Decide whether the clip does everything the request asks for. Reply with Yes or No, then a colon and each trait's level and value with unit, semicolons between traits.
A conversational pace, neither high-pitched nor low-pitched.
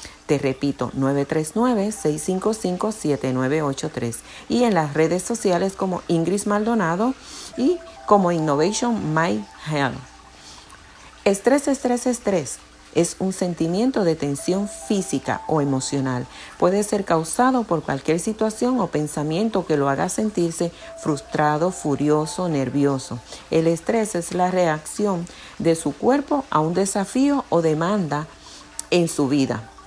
No: slow, 115 wpm; medium, 170 Hz